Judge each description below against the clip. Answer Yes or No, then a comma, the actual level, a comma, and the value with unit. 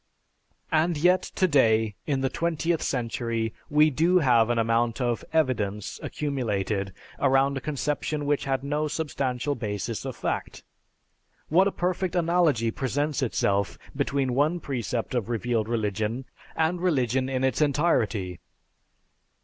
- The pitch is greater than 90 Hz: Yes, low, 135 Hz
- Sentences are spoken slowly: Yes, slow, 130 wpm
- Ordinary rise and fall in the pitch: Yes, average, 4.9 semitones